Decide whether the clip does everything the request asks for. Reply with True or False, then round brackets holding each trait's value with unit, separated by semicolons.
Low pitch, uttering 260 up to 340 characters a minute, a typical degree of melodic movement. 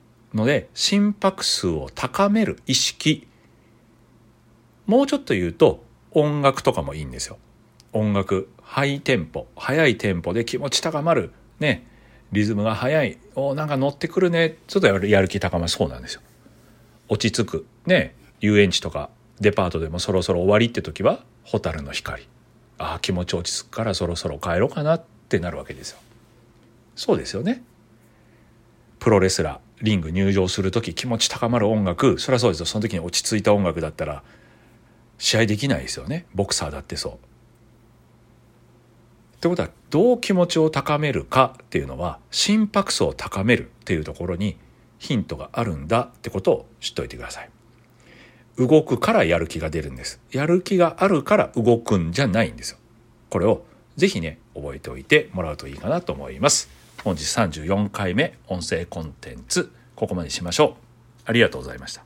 True (115 Hz; 280 characters per minute; 4.8 semitones)